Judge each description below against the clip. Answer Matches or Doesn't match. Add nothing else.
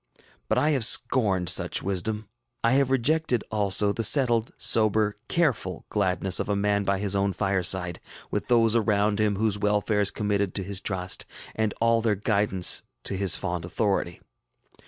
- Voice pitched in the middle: Doesn't match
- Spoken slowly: Doesn't match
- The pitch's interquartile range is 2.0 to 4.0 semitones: Matches